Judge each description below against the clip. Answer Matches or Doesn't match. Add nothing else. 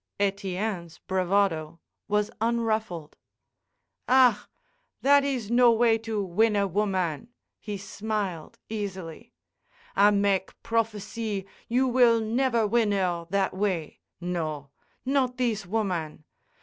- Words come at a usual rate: Doesn't match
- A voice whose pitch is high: Matches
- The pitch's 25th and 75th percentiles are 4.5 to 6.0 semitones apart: Doesn't match